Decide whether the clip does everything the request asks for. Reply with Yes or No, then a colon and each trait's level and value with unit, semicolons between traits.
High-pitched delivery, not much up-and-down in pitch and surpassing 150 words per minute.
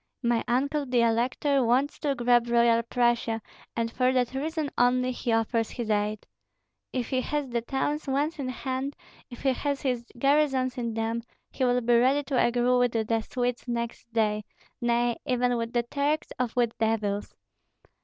Yes: high, 245 Hz; narrow, 2.3 semitones; average, 175 wpm